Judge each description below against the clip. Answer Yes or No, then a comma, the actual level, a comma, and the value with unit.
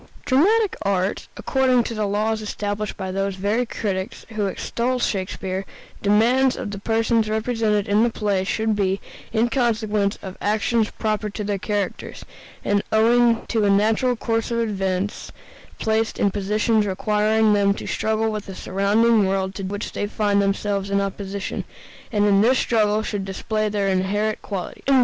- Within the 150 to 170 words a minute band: Yes, average, 160 wpm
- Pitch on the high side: Yes, high, 210 Hz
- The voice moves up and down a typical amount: No, narrow, 2.0 semitones